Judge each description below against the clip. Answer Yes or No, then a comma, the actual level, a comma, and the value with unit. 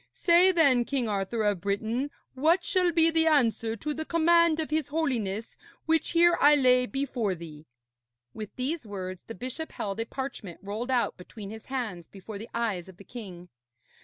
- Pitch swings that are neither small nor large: No, wide, 7.4 semitones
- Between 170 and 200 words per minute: Yes, average, 180 wpm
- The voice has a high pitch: Yes, high, 245 Hz